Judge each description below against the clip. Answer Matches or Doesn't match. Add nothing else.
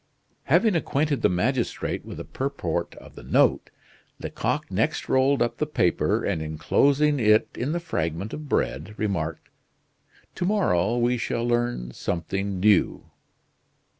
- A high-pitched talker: Doesn't match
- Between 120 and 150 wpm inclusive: Matches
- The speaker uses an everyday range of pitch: Doesn't match